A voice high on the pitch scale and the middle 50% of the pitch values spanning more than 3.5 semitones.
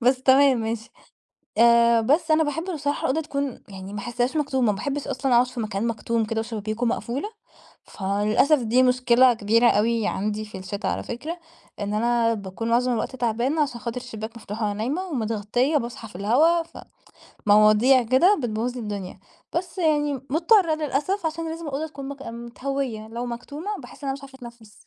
Yes: high, 240 Hz; average, 4.2 semitones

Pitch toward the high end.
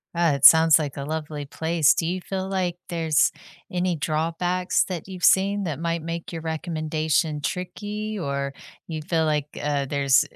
No: medium, 165 Hz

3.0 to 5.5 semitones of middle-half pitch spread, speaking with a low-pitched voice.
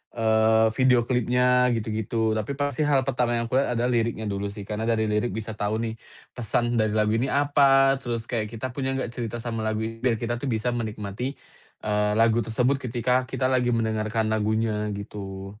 No: narrow, 2.5 semitones; low, 115 Hz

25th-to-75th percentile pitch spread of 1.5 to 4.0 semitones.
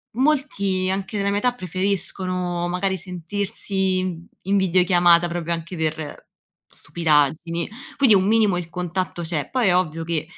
Yes: average, 2.7 semitones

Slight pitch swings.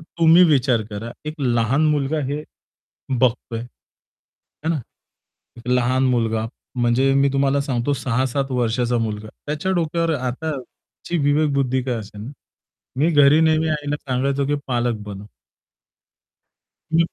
No: average, 3.7 semitones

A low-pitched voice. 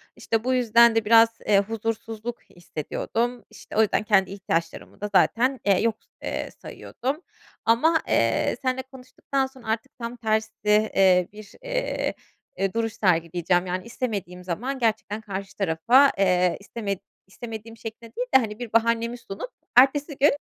No: high, 225 Hz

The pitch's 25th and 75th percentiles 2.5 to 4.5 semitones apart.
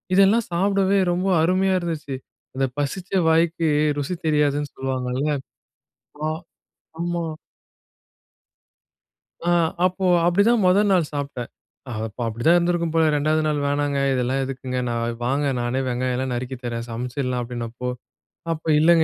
No: average, 5.3 semitones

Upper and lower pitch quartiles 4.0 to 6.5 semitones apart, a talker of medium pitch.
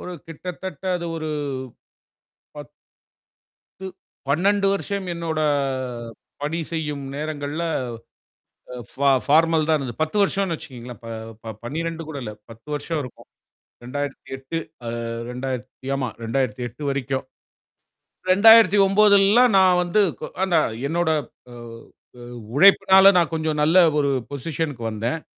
Yes: average, 5.1 semitones; medium, 155 Hz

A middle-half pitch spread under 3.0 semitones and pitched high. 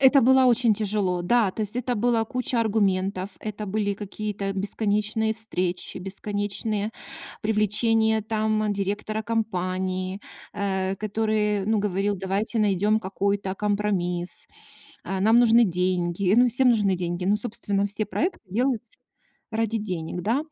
Yes: narrow, 2.4 semitones; high, 210 Hz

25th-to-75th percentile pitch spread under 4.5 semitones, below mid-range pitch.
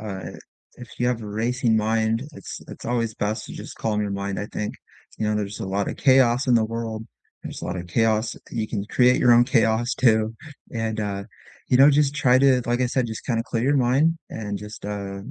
Yes: average, 2.7 semitones; low, 115 Hz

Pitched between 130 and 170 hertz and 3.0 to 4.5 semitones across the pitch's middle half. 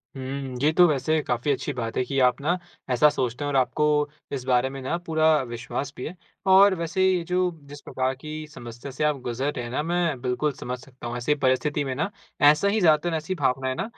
Yes: medium, 140 Hz; average, 3.6 semitones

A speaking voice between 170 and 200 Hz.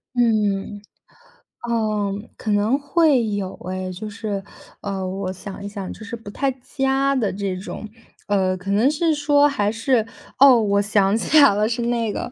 No: high, 215 Hz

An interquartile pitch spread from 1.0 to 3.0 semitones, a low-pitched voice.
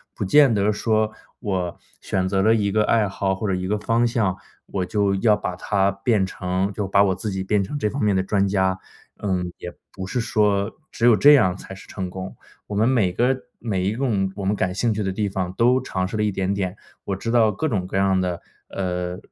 Yes: narrow, 2.4 semitones; low, 100 Hz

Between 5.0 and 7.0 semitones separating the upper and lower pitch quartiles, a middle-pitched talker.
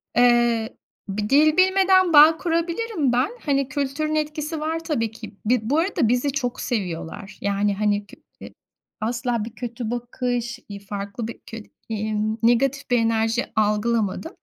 No: wide, 5.5 semitones; high, 245 Hz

